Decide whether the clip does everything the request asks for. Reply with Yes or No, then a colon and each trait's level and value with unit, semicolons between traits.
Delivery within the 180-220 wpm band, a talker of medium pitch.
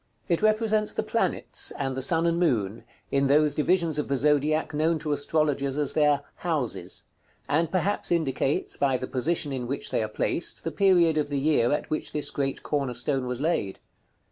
Yes: average, 190 wpm; medium, 150 Hz